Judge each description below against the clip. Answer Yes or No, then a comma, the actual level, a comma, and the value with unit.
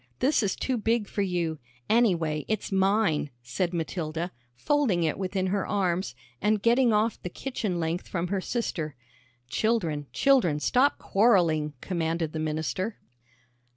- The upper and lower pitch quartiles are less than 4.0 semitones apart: No, average, 5.2 semitones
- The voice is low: No, medium, 185 Hz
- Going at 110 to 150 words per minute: Yes, average, 140 wpm